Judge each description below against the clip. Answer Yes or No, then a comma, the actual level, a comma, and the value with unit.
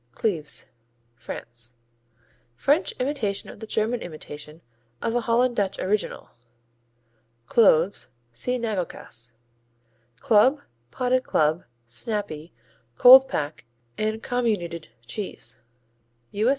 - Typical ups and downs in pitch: No, wide, 7.4 semitones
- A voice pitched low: No, high, 210 Hz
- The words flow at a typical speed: No, slow, 95 wpm